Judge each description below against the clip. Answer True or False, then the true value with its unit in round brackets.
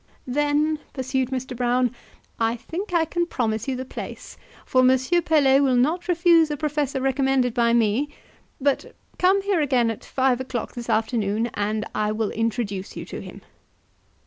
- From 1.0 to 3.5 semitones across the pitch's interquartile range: False (4.0 semitones)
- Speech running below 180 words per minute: True (165 wpm)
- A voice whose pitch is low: False (260 Hz)